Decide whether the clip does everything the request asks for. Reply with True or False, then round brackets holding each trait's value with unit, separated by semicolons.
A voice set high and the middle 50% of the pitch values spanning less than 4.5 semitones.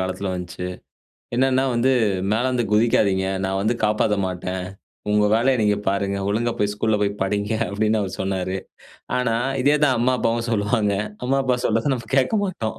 False (110 Hz; 3.9 semitones)